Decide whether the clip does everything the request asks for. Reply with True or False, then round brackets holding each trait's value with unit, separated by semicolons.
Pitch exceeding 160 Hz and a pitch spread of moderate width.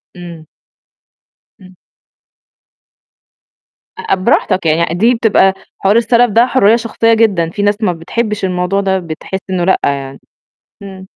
True (190 Hz; 3.9 semitones)